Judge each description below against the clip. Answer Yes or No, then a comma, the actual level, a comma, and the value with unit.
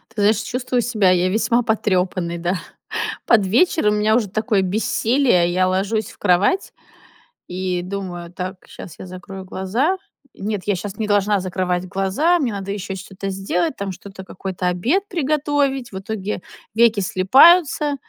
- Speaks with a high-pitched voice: Yes, high, 200 Hz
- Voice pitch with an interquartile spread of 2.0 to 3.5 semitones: No, average, 4.0 semitones